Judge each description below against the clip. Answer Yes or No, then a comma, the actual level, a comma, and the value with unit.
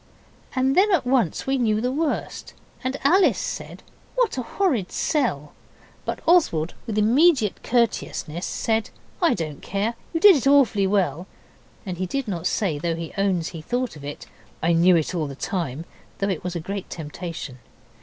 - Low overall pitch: No, high, 200 Hz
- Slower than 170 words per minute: No, average, 175 wpm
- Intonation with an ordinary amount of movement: No, wide, 7.8 semitones